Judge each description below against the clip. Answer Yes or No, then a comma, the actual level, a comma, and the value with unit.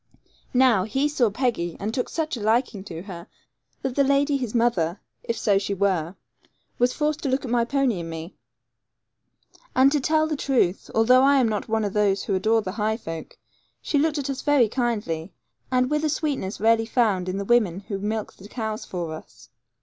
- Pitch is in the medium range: No, high, 225 Hz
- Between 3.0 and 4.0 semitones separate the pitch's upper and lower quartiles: No, average, 5.3 semitones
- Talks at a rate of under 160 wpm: No, average, 200 wpm